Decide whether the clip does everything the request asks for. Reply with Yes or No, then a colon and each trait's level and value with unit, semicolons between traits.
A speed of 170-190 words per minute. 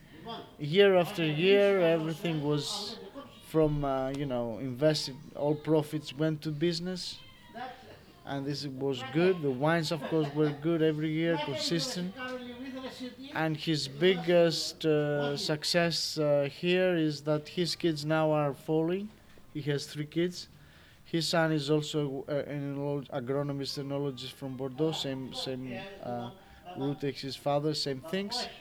No: slow, 135 wpm